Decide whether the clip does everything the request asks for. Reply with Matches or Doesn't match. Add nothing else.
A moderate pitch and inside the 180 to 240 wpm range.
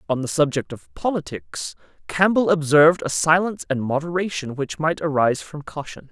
Doesn't match